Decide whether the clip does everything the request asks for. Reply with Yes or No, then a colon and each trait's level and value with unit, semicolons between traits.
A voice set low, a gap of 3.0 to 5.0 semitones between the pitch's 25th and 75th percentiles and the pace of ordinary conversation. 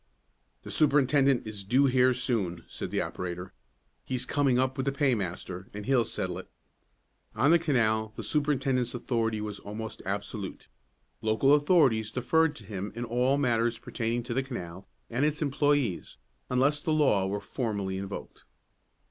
Yes: low, 120 Hz; average, 4.7 semitones; average, 155 wpm